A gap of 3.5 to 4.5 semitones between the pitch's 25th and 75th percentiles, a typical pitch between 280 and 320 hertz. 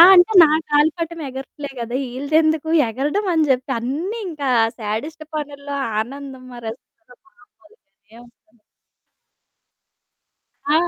Yes: average, 4.2 semitones; very high, 285 Hz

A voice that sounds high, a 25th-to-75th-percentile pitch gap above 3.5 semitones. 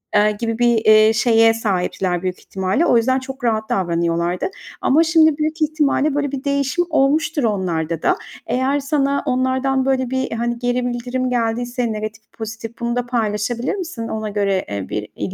Yes: high, 240 Hz; average, 4.0 semitones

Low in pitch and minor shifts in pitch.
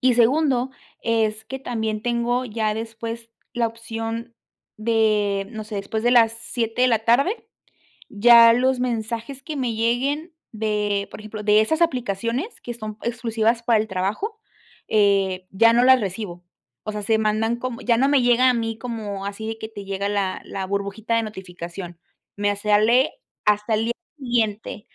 No: high, 225 Hz; narrow, 2.3 semitones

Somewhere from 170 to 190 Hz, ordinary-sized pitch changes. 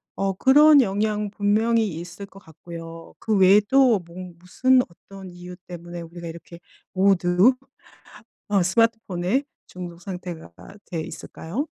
Yes: medium, 185 Hz; average, 3.6 semitones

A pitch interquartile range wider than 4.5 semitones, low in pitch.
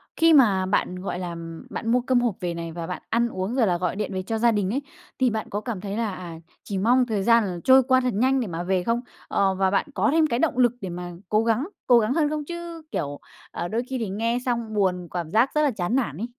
No: average, 5.1 semitones; high, 220 Hz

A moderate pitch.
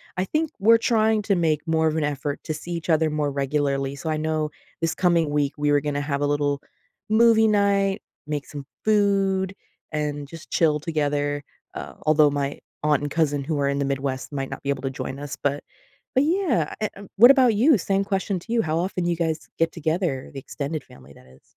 Yes: medium, 155 Hz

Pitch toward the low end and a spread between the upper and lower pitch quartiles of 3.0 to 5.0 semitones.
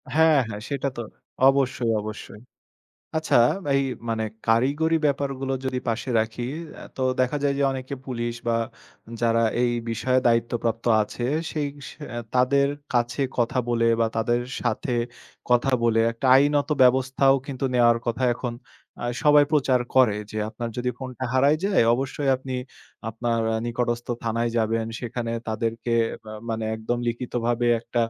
No: low, 120 Hz; narrow, 2.6 semitones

